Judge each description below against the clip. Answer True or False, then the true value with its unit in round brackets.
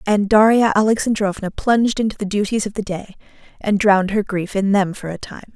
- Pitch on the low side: False (205 Hz)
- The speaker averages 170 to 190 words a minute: False (205 wpm)